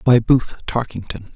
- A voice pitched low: Yes, low, 115 Hz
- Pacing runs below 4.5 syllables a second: Yes, 4.1 syllables/s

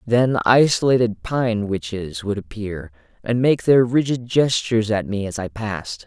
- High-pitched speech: No, low, 110 Hz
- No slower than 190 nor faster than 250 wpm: No, average, 160 wpm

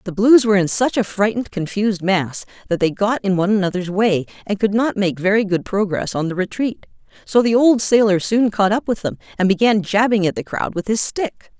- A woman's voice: Yes, female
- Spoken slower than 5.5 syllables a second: No, 5.6 syllables/s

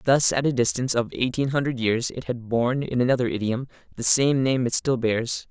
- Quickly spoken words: Yes, fast, 220 wpm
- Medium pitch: No, low, 125 Hz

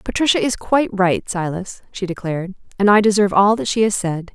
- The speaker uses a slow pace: No, fast, 205 wpm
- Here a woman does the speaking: Yes, female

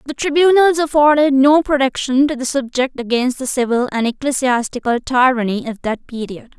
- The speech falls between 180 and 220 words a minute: No, average, 155 wpm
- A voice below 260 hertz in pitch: No, very high, 265 Hz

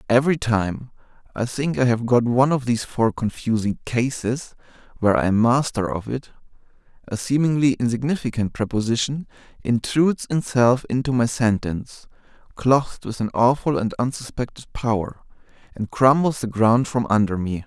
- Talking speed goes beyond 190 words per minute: No, average, 145 wpm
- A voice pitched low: Yes, low, 120 Hz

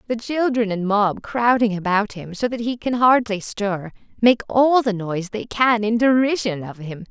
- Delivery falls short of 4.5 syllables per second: No, 4.6 syllables/s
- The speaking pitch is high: Yes, high, 220 Hz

